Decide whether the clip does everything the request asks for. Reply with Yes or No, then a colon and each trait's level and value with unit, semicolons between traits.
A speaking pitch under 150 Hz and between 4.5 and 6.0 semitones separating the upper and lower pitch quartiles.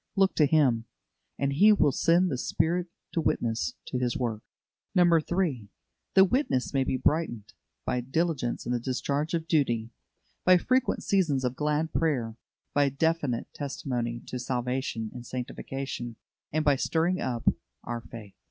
Yes: medium, 140 Hz; average, 5.0 semitones